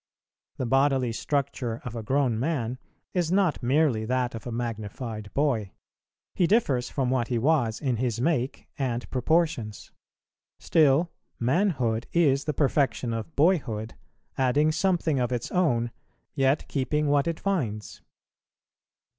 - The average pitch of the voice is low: Yes, low, 130 Hz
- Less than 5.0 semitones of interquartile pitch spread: Yes, average, 4.5 semitones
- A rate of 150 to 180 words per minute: No, slow, 135 wpm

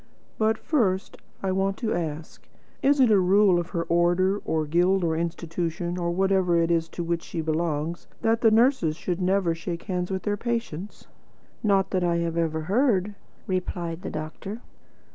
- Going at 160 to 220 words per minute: Yes, average, 175 wpm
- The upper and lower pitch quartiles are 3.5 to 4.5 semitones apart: No, average, 2.9 semitones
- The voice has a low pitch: No, medium, 180 Hz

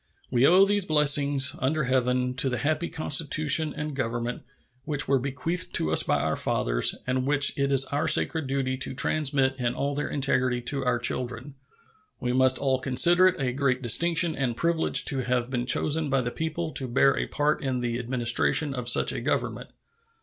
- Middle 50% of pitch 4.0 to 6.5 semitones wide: No, average, 2.9 semitones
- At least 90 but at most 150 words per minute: No, average, 190 wpm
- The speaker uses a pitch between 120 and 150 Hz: Yes, low, 135 Hz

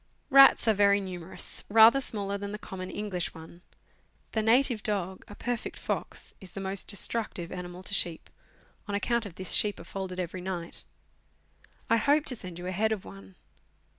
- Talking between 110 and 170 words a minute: No, average, 180 wpm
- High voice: Yes, high, 195 Hz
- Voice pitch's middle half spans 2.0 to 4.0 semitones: Yes, average, 3.3 semitones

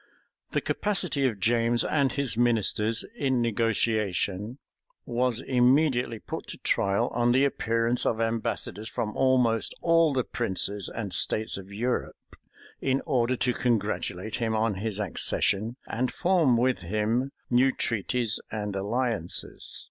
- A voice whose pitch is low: Yes, low, 115 Hz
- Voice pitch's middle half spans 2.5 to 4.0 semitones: Yes, average, 2.9 semitones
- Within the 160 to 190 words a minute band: No, slow, 135 wpm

